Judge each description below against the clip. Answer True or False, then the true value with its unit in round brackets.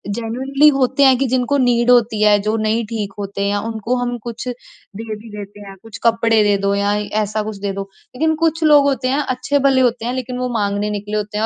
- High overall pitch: True (230 Hz)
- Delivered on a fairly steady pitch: False (3.5 semitones)